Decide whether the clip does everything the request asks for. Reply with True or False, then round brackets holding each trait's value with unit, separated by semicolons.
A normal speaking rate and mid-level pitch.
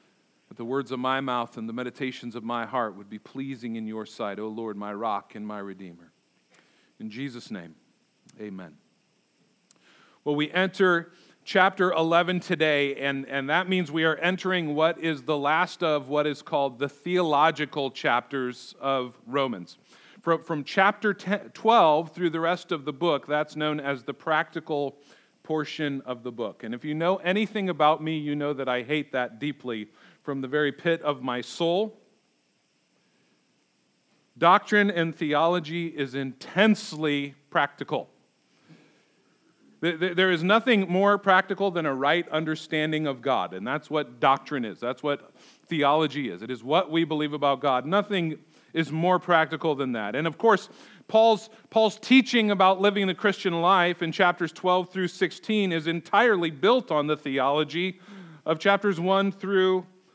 True (160 wpm; 155 Hz)